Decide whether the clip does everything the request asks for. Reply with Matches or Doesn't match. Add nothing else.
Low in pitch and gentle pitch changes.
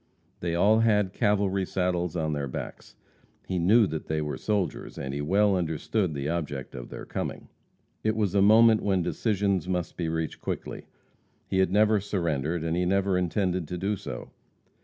Doesn't match